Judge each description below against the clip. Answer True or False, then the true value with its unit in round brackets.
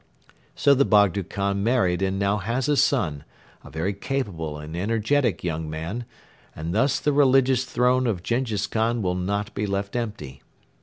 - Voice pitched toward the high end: False (105 Hz)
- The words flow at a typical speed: True (165 wpm)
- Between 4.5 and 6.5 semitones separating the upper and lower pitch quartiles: True (5.4 semitones)